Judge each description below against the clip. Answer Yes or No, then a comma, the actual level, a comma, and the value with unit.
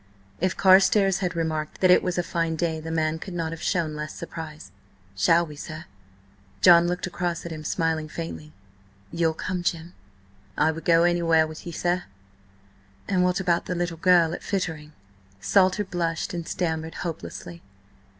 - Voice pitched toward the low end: No, medium, 170 Hz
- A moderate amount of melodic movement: No, narrow, 1.8 semitones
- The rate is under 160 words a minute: No, average, 170 wpm